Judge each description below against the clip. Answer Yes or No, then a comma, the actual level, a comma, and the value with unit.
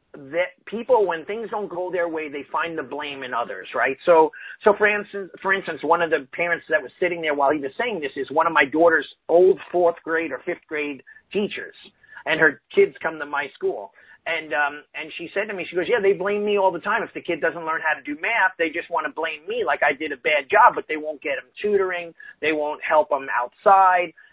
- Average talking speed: No, fast, 250 wpm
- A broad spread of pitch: No, average, 4.4 semitones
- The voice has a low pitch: No, medium, 170 Hz